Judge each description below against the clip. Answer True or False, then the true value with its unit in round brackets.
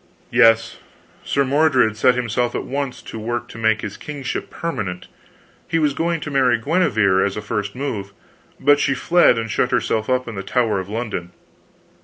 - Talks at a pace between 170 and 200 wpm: True (180 wpm)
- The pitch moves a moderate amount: True (4.5 semitones)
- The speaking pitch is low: True (120 Hz)